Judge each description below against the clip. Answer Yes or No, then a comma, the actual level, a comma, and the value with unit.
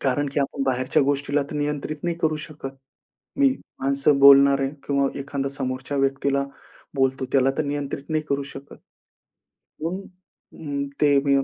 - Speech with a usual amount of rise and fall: No, narrow, 1.2 semitones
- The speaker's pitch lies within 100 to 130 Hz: No, medium, 140 Hz